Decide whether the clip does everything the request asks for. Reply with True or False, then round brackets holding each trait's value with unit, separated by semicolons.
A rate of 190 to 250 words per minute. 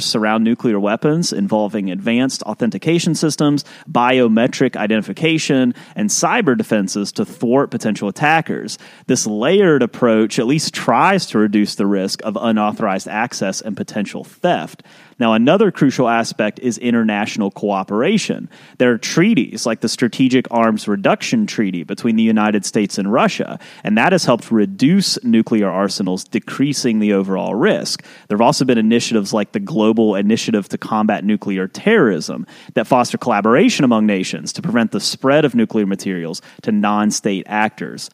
False (150 wpm)